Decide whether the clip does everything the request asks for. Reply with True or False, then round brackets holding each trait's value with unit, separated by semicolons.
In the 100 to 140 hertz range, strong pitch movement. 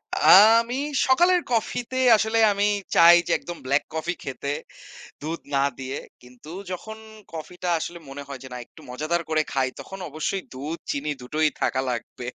False (155 Hz; 6.1 semitones)